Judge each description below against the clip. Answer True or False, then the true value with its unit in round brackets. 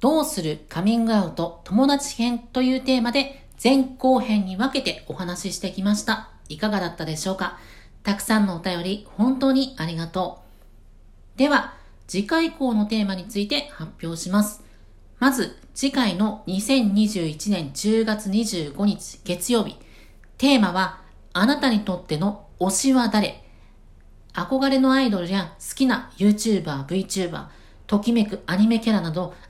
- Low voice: False (210 Hz)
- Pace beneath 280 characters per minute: False (300 characters per minute)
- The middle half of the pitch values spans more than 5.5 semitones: False (5.2 semitones)